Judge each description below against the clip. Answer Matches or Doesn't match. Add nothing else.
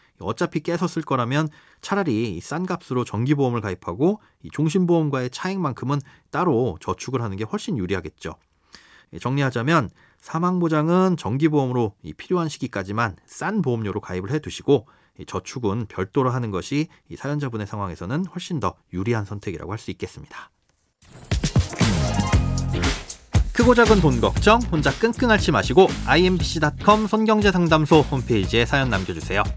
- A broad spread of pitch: Matches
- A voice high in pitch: Doesn't match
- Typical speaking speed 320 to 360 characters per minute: Matches